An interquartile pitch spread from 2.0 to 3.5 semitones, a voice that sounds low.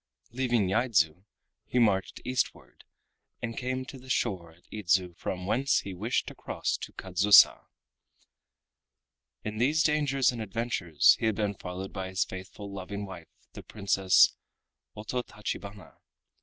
No: average, 4.4 semitones; low, 100 Hz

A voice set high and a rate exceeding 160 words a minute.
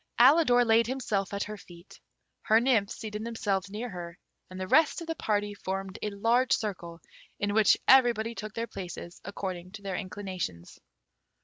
Yes: high, 205 Hz; average, 170 wpm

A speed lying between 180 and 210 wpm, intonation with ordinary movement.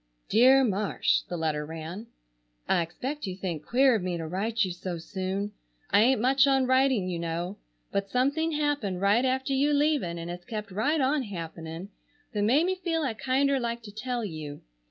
No: average, 185 wpm; wide, 6.8 semitones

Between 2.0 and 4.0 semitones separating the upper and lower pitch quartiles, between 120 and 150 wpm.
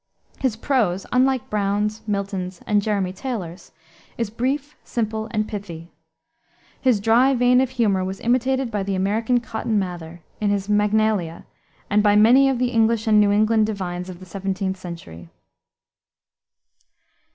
Yes: average, 3.4 semitones; average, 145 wpm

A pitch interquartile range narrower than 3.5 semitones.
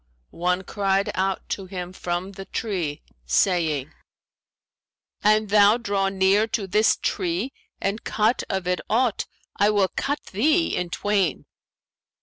Yes: average, 2.8 semitones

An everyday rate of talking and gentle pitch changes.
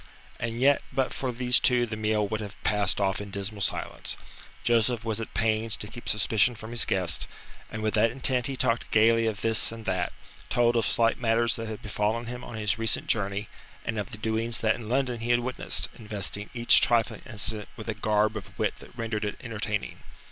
No: fast, 210 wpm; narrow, 1.9 semitones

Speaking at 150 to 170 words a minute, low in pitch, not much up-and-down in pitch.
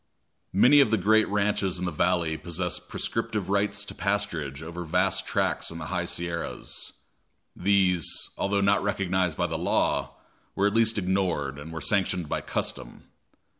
No: average, 160 wpm; very low, 95 Hz; average, 3.2 semitones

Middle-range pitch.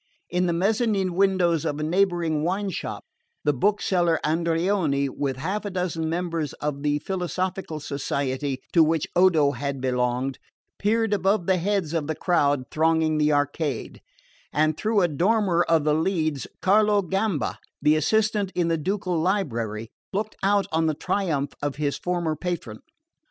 Yes: medium, 165 Hz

